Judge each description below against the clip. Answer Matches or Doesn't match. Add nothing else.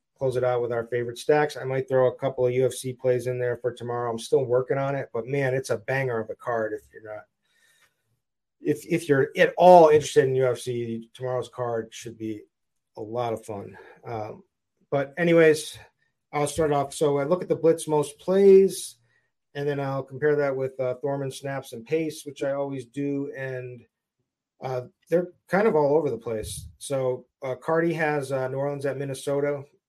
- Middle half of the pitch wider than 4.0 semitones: Doesn't match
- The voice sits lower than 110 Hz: Doesn't match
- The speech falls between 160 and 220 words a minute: Matches